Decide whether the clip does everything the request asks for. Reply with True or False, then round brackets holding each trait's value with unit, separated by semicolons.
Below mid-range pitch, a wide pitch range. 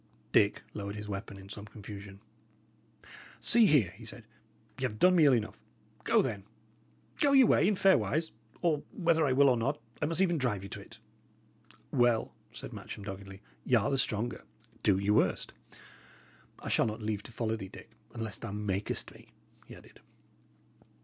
True (110 Hz; 6.2 semitones)